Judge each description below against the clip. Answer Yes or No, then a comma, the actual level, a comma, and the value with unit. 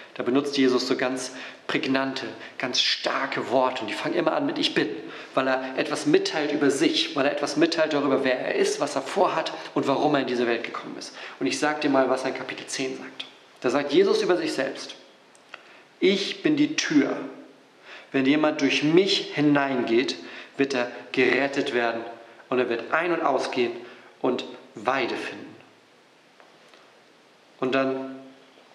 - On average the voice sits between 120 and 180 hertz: Yes, low, 135 Hz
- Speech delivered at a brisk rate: No, average, 175 wpm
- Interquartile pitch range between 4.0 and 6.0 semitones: No, average, 2.9 semitones